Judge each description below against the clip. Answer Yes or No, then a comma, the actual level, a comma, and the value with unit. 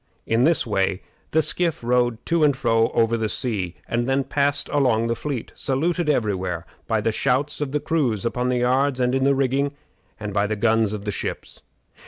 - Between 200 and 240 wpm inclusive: Yes, fast, 205 wpm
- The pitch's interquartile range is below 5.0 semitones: Yes, average, 4.1 semitones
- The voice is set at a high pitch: No, low, 125 Hz